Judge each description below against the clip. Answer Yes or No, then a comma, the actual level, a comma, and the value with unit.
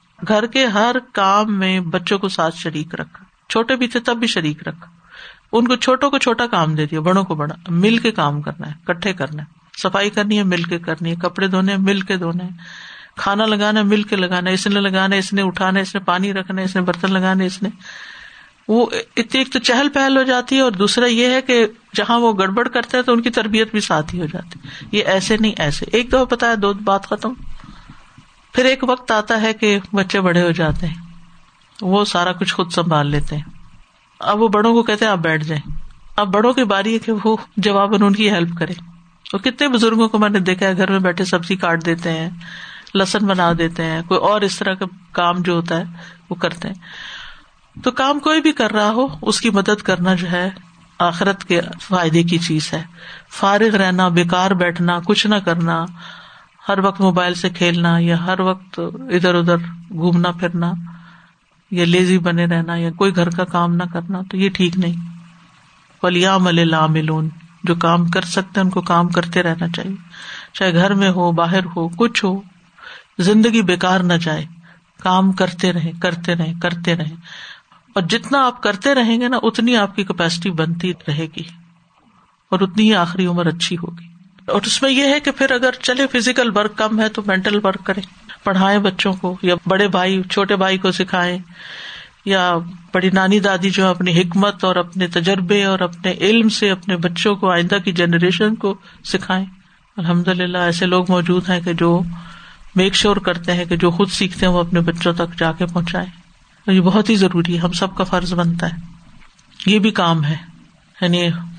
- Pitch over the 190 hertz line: No, medium, 185 Hz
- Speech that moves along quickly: Yes, fast, 200 wpm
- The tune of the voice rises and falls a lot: No, average, 3.1 semitones